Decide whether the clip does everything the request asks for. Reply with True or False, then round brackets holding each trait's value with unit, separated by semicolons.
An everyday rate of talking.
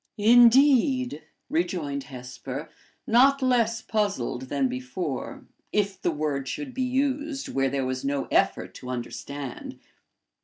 False (120 wpm)